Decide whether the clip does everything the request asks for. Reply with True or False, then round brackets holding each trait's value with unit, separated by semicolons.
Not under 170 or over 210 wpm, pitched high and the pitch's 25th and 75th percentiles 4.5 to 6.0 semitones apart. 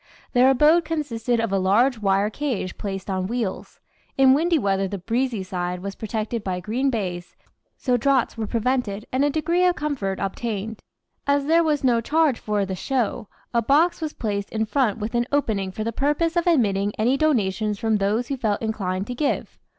True (190 wpm; 230 Hz; 5.5 semitones)